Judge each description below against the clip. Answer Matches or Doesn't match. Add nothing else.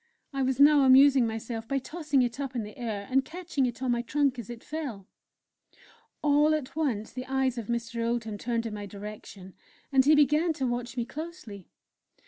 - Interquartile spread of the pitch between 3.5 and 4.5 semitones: Matches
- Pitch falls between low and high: Doesn't match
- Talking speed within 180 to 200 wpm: Matches